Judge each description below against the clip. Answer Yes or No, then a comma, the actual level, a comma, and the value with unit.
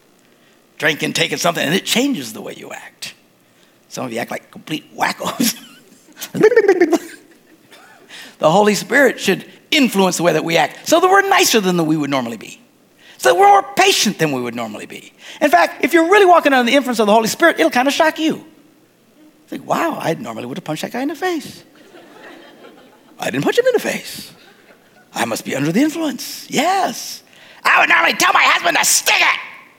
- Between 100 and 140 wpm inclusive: No, average, 200 wpm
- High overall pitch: Yes, very high, 285 Hz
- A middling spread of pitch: No, wide, 8.4 semitones